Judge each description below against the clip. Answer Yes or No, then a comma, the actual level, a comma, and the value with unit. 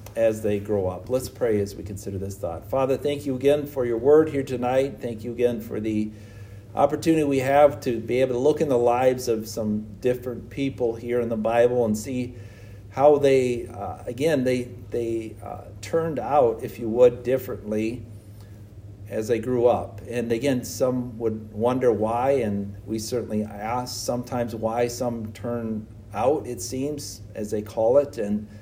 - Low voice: Yes, low, 115 Hz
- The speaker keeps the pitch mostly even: No, average, 3.1 semitones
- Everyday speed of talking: Yes, average, 180 wpm